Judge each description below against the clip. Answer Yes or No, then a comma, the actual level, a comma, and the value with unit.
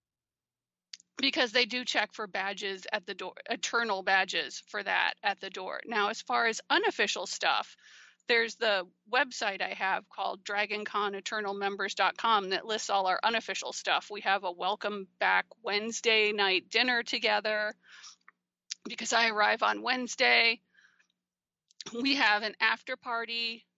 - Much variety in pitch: No, average, 2.9 semitones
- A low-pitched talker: No, high, 215 Hz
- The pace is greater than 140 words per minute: No, slow, 135 wpm